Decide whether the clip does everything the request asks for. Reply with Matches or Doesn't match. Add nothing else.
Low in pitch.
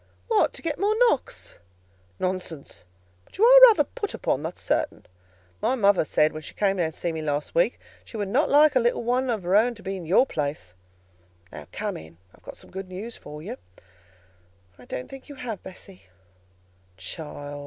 Doesn't match